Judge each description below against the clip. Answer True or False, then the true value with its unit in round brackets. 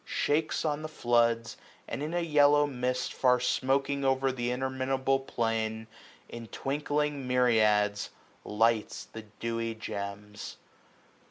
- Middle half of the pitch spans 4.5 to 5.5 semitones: False (3.6 semitones)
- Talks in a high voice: False (125 Hz)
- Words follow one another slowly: True (115 wpm)